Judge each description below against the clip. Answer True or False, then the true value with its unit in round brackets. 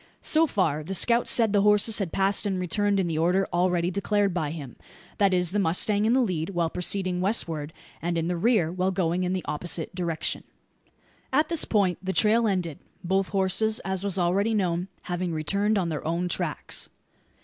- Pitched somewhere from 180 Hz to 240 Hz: True (185 Hz)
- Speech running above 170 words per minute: True (195 wpm)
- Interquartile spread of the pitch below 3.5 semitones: True (2.9 semitones)